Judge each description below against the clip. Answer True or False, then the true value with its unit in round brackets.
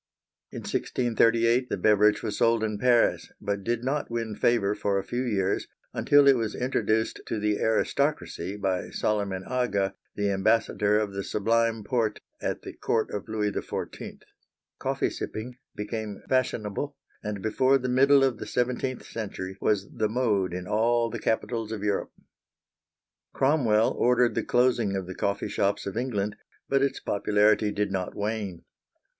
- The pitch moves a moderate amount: True (3.0 semitones)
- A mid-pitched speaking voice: False (110 Hz)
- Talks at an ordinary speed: True (155 wpm)